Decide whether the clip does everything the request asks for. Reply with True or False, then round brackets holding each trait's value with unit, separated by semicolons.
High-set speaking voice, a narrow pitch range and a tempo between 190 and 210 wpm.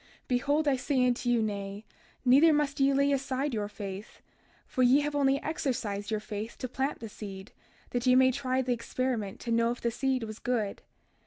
False (250 Hz; 3.8 semitones; 200 wpm)